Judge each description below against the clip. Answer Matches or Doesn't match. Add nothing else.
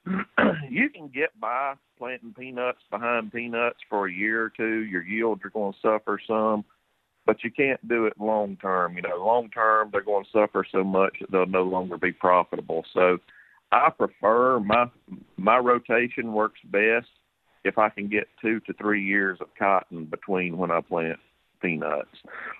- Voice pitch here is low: Matches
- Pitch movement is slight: Doesn't match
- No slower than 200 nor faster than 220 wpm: Doesn't match